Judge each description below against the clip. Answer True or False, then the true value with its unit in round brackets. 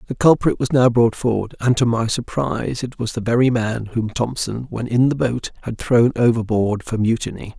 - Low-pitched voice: True (115 Hz)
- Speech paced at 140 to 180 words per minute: False (205 wpm)